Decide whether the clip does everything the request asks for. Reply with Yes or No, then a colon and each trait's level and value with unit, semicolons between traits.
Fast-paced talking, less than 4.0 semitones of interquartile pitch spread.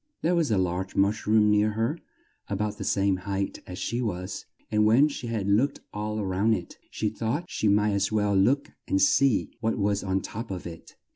Yes: fast, 215 wpm; narrow, 2.5 semitones